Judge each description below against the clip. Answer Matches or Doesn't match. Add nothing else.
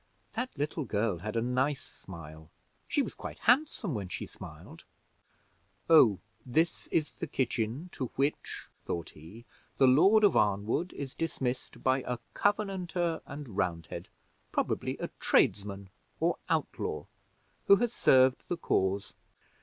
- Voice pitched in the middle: Doesn't match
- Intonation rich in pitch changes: Matches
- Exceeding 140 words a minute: Doesn't match